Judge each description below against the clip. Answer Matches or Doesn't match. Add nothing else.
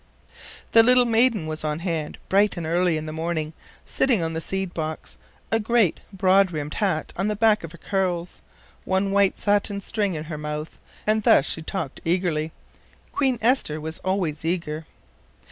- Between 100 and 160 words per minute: Doesn't match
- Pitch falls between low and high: Matches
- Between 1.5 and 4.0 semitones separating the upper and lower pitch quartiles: Doesn't match